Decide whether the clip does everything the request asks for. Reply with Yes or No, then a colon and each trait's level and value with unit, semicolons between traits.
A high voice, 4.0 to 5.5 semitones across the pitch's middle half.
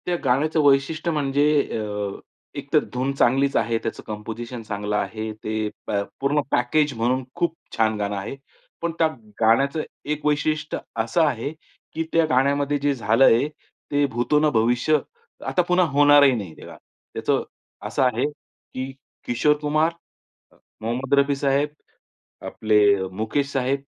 No: low, 135 Hz; average, 4.5 semitones